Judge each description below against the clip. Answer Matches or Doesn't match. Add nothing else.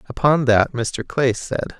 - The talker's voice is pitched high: Doesn't match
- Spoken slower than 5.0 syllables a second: Matches